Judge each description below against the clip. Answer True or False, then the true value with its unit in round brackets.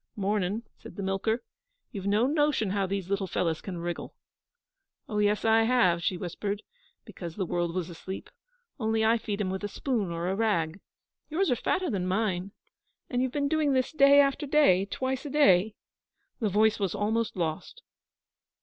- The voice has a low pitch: False (205 Hz)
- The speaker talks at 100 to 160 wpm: False (175 wpm)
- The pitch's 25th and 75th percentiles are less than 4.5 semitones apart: False (4.9 semitones)